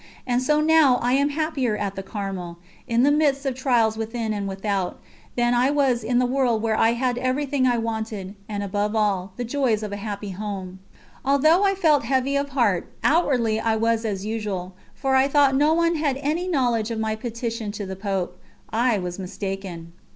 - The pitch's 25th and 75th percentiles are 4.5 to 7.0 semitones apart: Yes, average, 4.8 semitones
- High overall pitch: Yes, high, 230 Hz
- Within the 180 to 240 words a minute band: Yes, average, 195 wpm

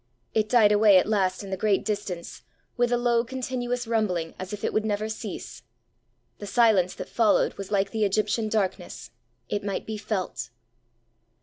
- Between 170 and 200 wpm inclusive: Yes, average, 175 wpm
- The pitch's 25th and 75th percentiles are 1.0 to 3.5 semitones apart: Yes, narrow, 2.4 semitones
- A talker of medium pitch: No, high, 210 Hz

